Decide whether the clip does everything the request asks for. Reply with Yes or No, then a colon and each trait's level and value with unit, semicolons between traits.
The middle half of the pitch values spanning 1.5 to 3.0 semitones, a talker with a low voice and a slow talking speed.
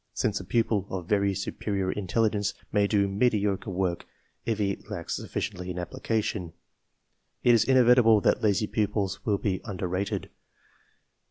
No: narrow, 2.4 semitones; low, 100 Hz; average, 165 wpm